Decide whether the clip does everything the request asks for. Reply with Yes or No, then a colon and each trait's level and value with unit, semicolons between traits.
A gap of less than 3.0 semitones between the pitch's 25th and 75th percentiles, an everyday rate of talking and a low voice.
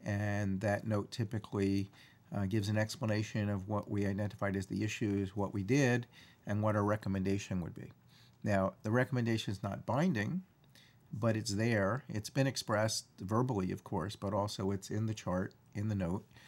Yes: narrow, 2.4 semitones; average, 175 wpm; low, 105 Hz